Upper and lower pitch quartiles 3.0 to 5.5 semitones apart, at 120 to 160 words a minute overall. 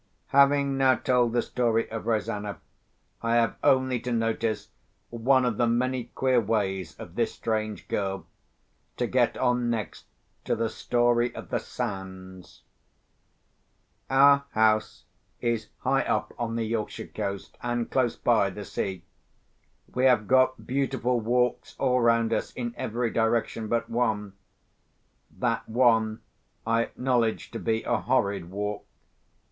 No: narrow, 2.4 semitones; average, 140 wpm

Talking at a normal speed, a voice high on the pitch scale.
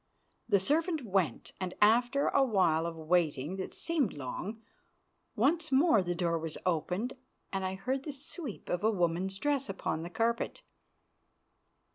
Yes: average, 150 wpm; high, 195 Hz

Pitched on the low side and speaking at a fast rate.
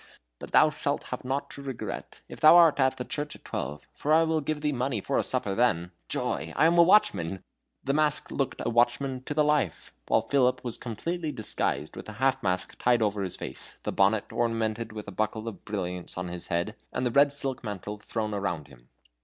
Yes: low, 120 Hz; fast, 220 wpm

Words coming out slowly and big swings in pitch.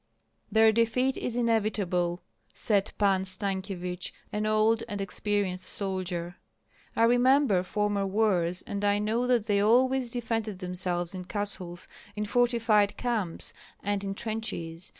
No: slow, 130 wpm; average, 3.3 semitones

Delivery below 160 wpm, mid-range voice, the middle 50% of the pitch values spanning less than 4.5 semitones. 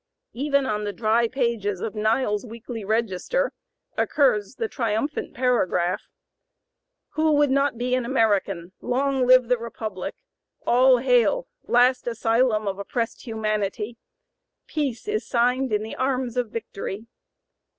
No: slow, 135 wpm; high, 235 Hz; average, 3.4 semitones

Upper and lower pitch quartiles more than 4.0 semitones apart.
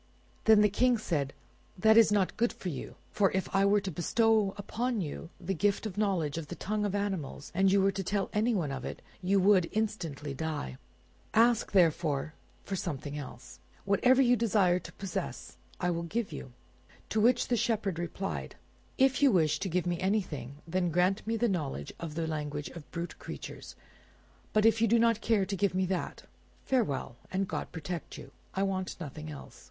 Yes: average, 4.6 semitones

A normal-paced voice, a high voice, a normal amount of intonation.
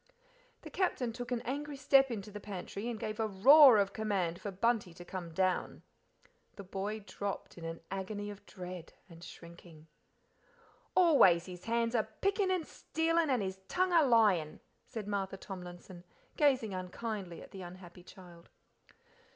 Yes: average, 160 wpm; high, 205 Hz; average, 4.8 semitones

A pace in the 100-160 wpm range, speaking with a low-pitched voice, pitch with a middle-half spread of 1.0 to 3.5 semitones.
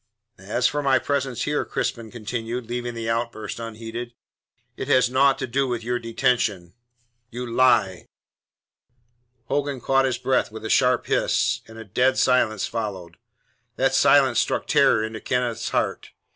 Yes: average, 150 wpm; low, 120 Hz; narrow, 2.4 semitones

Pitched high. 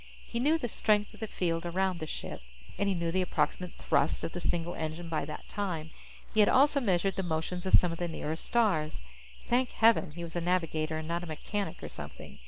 No: medium, 175 Hz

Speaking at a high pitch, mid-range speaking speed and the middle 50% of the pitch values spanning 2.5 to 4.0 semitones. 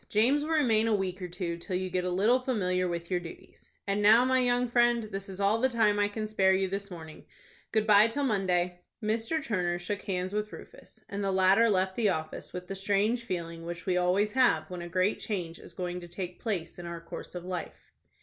No: high, 195 Hz; fast, 230 wpm; average, 3.4 semitones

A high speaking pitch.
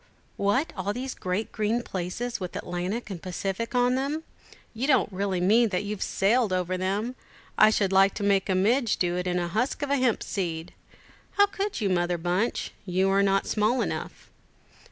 Yes: high, 200 Hz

